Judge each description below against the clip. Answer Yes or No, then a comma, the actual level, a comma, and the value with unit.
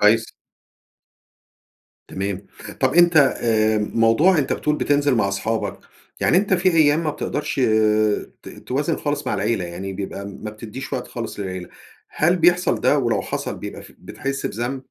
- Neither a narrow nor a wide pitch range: No, wide, 6.2 semitones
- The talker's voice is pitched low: Yes, low, 120 Hz